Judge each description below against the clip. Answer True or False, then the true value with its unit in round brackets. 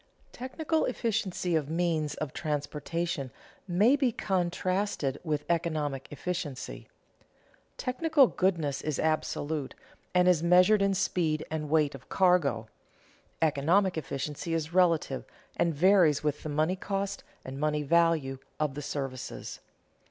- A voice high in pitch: False (165 Hz)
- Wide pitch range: False (3.9 semitones)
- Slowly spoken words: True (120 wpm)